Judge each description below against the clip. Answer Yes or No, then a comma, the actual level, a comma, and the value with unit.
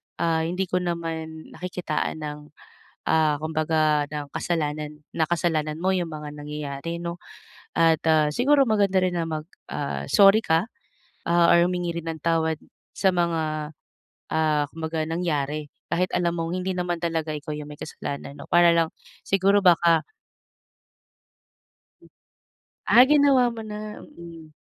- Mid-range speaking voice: Yes, medium, 165 Hz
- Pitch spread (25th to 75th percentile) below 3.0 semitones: Yes, narrow, 2.5 semitones